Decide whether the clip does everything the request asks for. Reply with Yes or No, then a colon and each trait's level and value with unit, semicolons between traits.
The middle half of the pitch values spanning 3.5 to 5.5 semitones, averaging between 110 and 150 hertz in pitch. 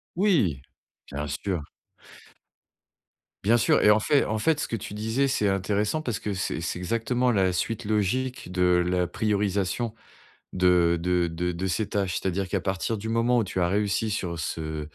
No: average, 3.9 semitones; low, 100 Hz